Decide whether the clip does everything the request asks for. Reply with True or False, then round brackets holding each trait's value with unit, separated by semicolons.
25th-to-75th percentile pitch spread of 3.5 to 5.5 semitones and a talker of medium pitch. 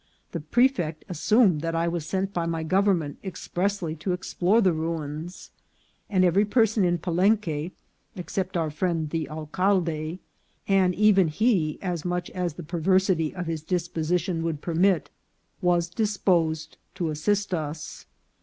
False (3.0 semitones; 175 Hz)